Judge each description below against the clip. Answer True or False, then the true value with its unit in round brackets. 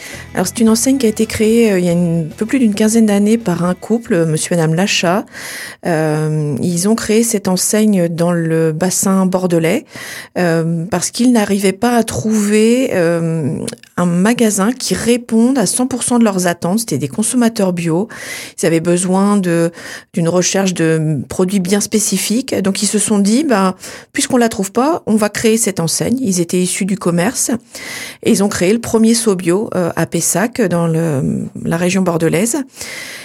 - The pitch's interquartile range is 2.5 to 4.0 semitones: False (4.4 semitones)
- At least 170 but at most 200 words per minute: True (180 wpm)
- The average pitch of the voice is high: True (195 Hz)